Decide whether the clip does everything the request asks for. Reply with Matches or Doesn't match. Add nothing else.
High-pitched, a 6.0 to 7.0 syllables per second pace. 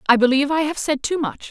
Matches